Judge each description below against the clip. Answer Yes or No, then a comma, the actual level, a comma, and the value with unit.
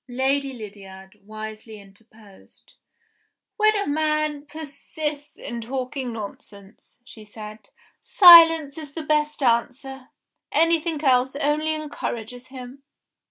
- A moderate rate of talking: No, slow, 105 wpm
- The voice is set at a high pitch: Yes, very high, 270 Hz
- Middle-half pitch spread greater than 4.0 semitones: Yes, wide, 5.4 semitones